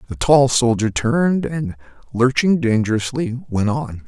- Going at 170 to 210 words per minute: No, slow, 135 wpm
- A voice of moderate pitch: No, low, 125 Hz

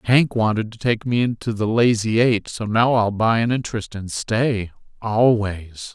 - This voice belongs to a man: Yes, male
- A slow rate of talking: No, average, 170 wpm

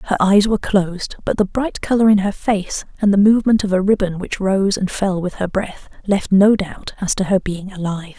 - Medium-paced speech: No, fast, 235 wpm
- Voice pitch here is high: Yes, high, 195 Hz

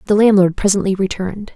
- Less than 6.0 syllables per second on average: No, 6.6 syllables/s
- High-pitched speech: Yes, high, 195 Hz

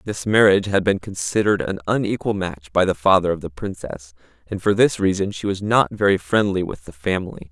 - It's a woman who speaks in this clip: No, male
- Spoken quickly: Yes, fast, 210 wpm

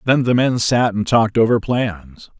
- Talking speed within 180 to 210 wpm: Yes, average, 200 wpm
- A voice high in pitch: No, low, 115 Hz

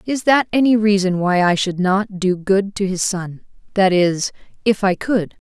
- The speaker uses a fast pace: No, average, 185 wpm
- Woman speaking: Yes, female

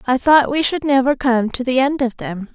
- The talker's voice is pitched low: No, very high, 260 Hz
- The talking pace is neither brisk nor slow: No, fast, 260 wpm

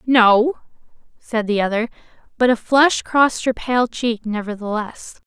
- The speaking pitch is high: Yes, high, 235 Hz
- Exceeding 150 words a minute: No, slow, 135 wpm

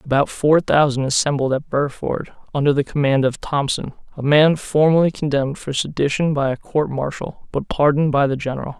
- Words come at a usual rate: Yes, average, 175 wpm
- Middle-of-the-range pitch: Yes, medium, 145 Hz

